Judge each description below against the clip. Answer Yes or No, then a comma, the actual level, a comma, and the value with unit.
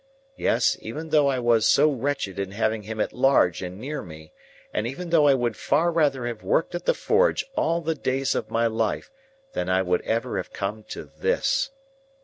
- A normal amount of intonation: No, wide, 6.1 semitones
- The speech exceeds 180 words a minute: Yes, average, 200 wpm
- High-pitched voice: No, low, 125 Hz